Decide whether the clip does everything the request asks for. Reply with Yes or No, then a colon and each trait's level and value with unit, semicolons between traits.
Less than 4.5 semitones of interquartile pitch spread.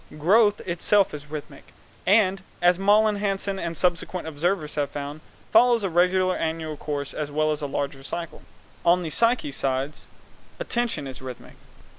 No: average, 4.9 semitones